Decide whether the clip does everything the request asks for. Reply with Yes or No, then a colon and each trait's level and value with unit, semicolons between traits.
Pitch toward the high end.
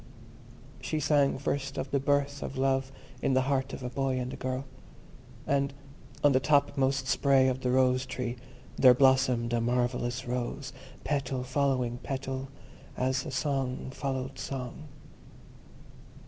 No: low, 130 Hz